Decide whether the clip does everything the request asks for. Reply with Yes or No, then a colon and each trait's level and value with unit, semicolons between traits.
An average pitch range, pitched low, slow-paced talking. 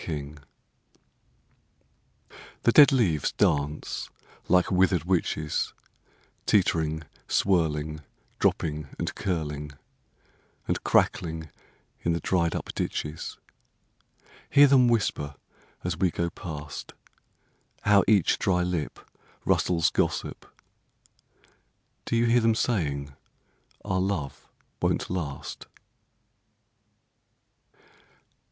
Yes: average, 4.1 semitones; very low, 85 Hz; slow, 75 wpm